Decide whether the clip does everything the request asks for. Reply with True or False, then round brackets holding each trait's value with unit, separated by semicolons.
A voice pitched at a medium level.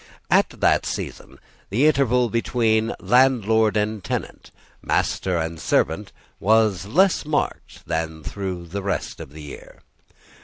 False (105 Hz)